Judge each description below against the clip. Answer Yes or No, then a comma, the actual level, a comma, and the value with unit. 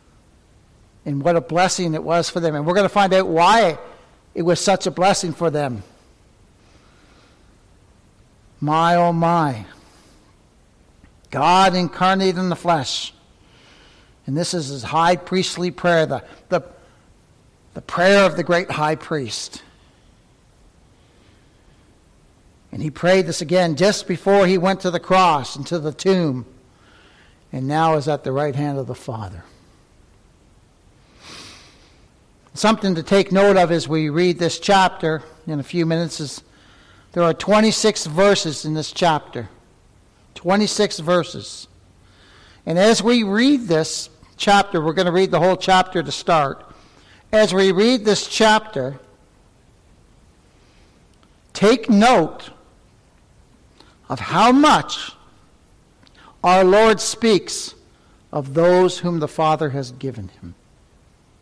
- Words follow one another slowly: Yes, slow, 130 wpm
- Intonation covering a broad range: No, average, 4.8 semitones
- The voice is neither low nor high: Yes, medium, 170 Hz